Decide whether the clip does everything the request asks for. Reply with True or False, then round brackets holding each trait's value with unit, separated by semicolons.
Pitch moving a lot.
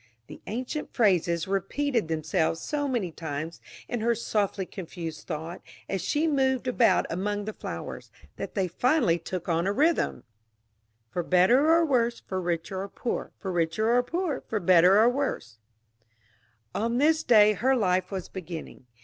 True (6.5 semitones)